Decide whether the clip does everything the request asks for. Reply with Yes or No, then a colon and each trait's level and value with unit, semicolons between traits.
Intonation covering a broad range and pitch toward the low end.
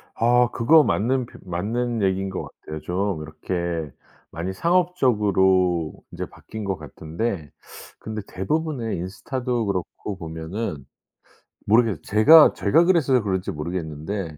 Yes: wide, 5.7 semitones; low, 100 Hz